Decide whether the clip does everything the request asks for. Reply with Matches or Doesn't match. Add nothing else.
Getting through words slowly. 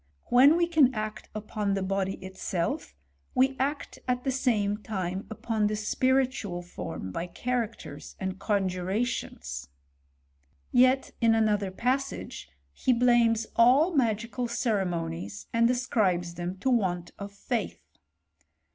Matches